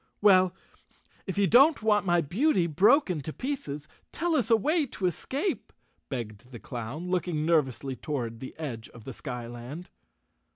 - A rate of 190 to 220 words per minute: No, average, 155 wpm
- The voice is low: No, medium, 170 Hz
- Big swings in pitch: Yes, wide, 8.4 semitones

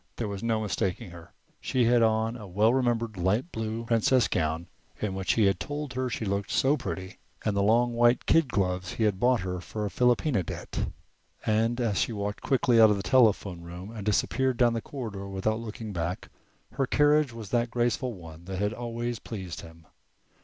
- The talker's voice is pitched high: No, low, 110 Hz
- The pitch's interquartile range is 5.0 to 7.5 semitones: No, average, 3.7 semitones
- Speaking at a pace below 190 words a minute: No, average, 200 wpm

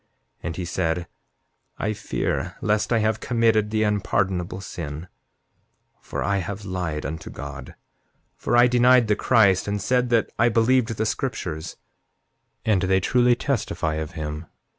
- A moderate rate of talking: Yes, average, 150 wpm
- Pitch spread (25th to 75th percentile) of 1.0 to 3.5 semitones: No, average, 4.9 semitones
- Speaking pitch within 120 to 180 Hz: No, low, 100 Hz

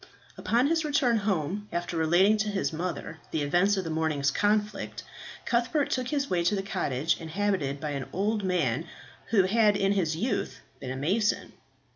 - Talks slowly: No, average, 175 wpm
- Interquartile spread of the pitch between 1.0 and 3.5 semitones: No, average, 4.9 semitones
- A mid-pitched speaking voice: No, high, 195 Hz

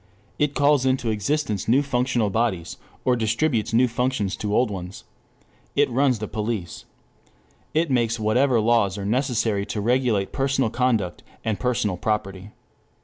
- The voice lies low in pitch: Yes, low, 115 Hz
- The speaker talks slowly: No, average, 145 wpm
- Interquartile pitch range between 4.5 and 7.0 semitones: No, average, 3.6 semitones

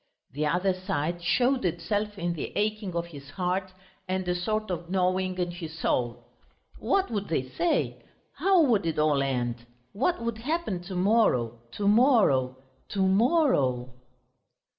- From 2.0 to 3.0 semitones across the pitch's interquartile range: No, average, 5.3 semitones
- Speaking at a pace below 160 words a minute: Yes, average, 150 wpm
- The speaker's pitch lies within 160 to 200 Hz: Yes, medium, 185 Hz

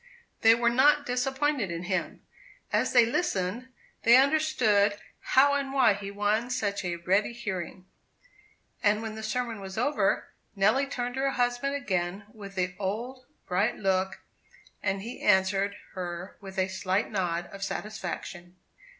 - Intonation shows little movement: No, average, 4.6 semitones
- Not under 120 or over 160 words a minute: Yes, average, 150 wpm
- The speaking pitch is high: Yes, high, 210 Hz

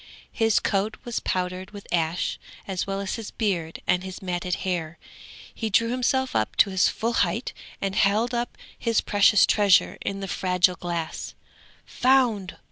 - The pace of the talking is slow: No, average, 160 wpm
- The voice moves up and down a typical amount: Yes, average, 3.6 semitones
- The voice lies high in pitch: Yes, high, 195 Hz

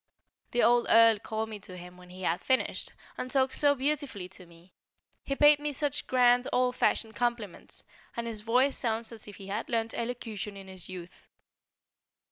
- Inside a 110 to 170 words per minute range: No, average, 190 wpm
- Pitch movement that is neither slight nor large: Yes, average, 4.4 semitones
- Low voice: No, high, 230 Hz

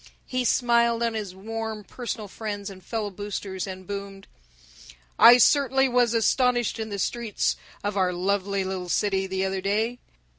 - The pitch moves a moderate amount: Yes, average, 3.4 semitones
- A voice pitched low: No, high, 205 Hz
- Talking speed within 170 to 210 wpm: No, average, 155 wpm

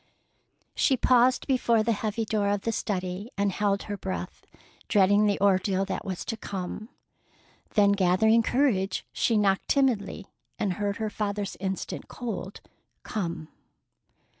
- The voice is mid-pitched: No, high, 205 Hz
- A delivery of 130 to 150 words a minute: Yes, average, 140 wpm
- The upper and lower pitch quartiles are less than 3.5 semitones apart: Yes, narrow, 2.4 semitones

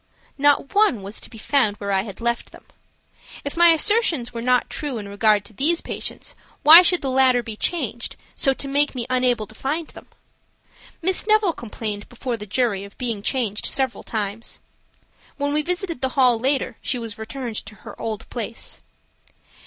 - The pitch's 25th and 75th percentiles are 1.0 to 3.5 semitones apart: No, average, 4.7 semitones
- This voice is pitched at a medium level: No, very high, 250 Hz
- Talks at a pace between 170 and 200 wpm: Yes, average, 185 wpm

